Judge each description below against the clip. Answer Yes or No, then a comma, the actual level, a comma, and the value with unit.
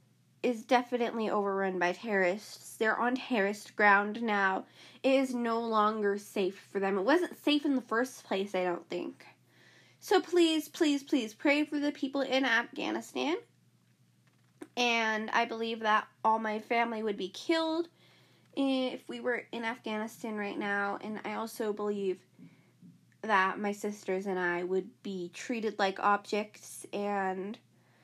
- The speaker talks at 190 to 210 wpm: No, average, 150 wpm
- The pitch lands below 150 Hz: No, high, 220 Hz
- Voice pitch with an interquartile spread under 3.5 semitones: No, average, 3.8 semitones